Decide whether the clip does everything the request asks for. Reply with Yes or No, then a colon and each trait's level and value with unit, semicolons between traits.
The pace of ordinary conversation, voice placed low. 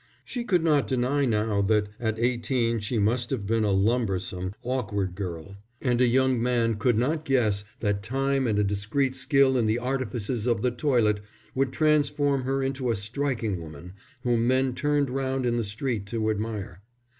Yes: average, 180 wpm; low, 120 Hz